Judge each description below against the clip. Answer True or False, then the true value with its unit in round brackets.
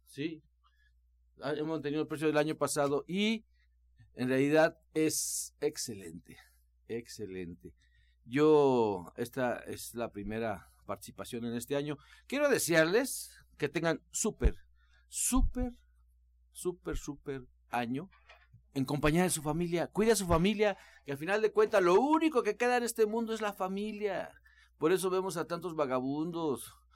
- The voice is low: False (150 Hz)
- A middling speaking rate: True (140 wpm)